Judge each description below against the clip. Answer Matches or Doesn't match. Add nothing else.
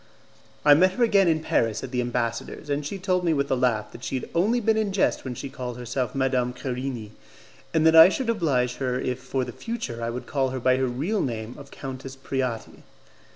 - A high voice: Doesn't match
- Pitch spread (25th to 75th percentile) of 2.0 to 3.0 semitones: Doesn't match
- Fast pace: Matches